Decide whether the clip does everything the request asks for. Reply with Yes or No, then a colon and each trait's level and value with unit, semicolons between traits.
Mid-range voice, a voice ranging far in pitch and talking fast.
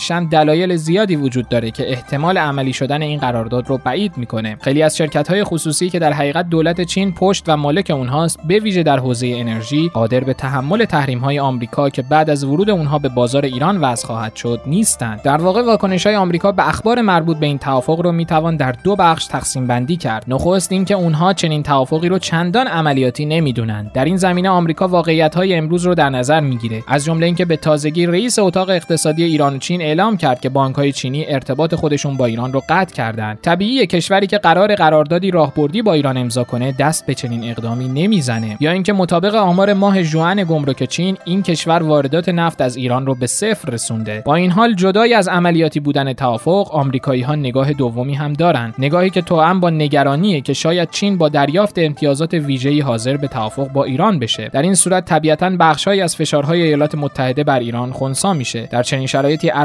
No: medium, 155 Hz; average, 4.8 semitones; fast, 195 wpm